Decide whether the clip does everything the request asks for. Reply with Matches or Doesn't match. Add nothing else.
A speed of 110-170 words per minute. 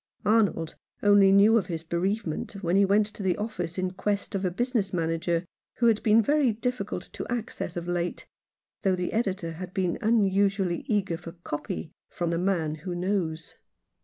Doesn't match